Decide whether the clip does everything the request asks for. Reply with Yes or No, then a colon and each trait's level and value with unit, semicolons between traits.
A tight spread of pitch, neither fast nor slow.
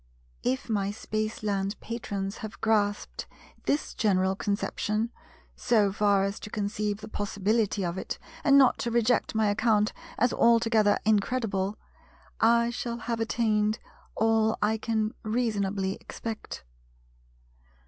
No: narrow, 1.9 semitones; slow, 120 wpm